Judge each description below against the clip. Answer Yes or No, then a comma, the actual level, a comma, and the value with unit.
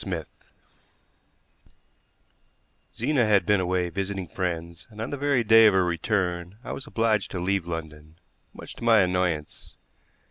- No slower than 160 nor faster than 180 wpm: No, average, 145 wpm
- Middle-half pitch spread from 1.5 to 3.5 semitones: No, average, 3.9 semitones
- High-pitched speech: No, very low, 95 Hz